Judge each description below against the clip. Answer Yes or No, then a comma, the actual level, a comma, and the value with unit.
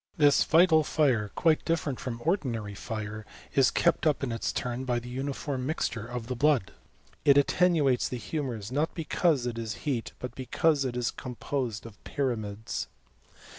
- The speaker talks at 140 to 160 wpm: No, average, 170 wpm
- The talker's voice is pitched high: No, low, 130 Hz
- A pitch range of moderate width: Yes, average, 4.3 semitones